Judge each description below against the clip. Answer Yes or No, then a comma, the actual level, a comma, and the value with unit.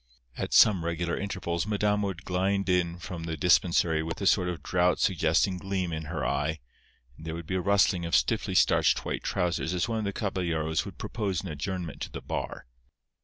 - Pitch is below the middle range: Yes, very low, 90 Hz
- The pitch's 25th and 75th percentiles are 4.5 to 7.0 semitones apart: No, average, 2.7 semitones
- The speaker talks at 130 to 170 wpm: No, average, 200 wpm